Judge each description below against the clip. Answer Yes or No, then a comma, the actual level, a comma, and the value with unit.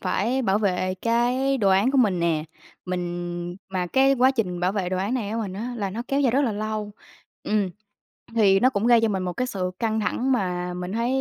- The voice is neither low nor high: No, high, 205 Hz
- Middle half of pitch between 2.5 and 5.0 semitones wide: Yes, average, 4.7 semitones